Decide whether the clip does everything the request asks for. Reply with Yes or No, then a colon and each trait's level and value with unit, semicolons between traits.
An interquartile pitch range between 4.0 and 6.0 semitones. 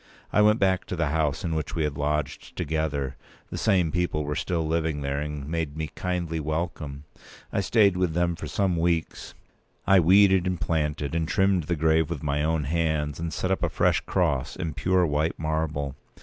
No: average, 2.9 semitones